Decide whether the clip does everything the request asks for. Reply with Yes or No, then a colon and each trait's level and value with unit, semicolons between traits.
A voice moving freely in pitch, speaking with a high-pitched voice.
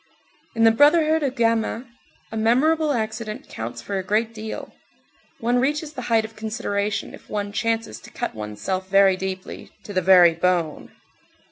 No: average, 3.9 semitones; high, 220 Hz